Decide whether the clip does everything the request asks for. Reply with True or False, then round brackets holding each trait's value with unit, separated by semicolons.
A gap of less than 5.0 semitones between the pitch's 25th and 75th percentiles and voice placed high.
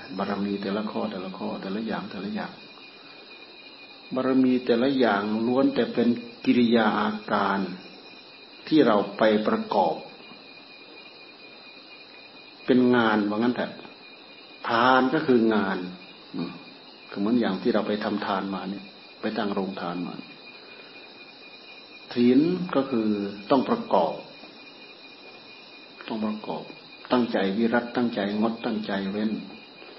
False (3.4 semitones; 110 Hz)